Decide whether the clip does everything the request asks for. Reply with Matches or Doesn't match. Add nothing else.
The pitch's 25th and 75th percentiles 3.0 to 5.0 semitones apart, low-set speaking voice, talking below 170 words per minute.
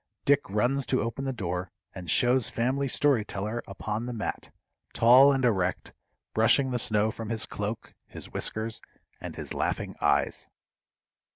Matches